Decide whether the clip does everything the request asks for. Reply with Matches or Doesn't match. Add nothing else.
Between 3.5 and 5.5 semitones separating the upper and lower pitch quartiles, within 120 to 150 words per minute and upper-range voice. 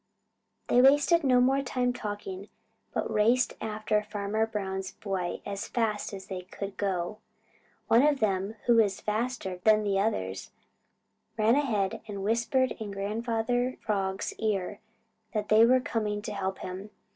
Doesn't match